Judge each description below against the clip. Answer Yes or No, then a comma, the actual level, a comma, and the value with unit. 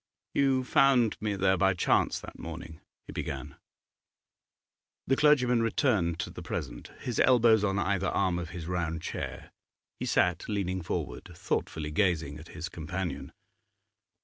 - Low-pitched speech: Yes, very low, 95 Hz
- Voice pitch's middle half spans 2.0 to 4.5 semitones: No, average, 5.3 semitones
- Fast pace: No, average, 145 wpm